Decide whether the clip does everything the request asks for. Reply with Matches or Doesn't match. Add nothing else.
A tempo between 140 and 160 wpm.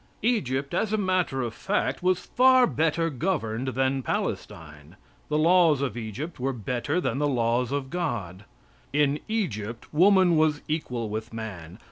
Matches